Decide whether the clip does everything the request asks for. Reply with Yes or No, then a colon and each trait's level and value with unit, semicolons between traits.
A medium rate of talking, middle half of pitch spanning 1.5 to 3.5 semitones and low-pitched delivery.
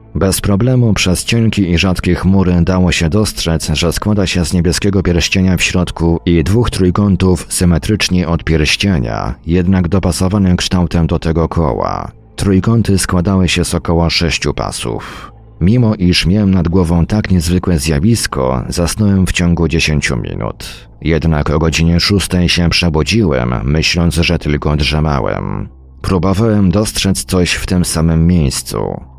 Yes: average, 140 wpm; average, 2.8 semitones; very low, 90 Hz